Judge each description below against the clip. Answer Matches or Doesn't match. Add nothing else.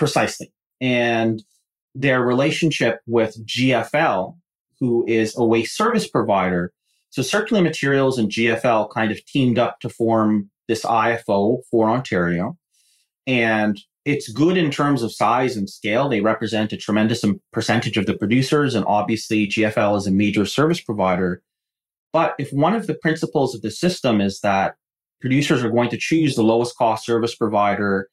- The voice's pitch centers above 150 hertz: Doesn't match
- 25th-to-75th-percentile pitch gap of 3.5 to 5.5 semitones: Matches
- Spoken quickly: Doesn't match